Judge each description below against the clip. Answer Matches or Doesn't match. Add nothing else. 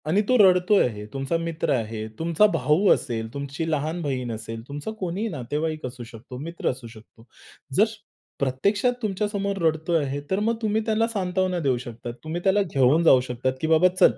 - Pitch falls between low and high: Matches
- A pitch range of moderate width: Doesn't match